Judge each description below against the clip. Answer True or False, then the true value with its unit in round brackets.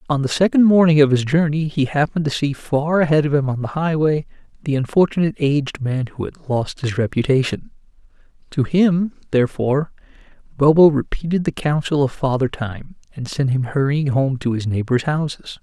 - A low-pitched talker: False (145 Hz)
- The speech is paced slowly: False (175 wpm)